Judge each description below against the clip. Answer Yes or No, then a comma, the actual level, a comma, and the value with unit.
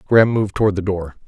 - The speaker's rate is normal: No, fast, 235 wpm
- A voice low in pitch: Yes, low, 100 Hz